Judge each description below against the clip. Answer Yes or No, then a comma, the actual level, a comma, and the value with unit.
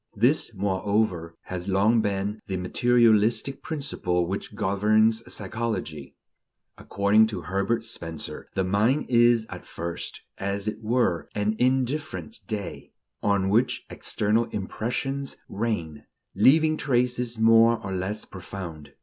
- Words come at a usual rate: No, slow, 115 wpm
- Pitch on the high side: No, low, 105 Hz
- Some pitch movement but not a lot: Yes, average, 3.5 semitones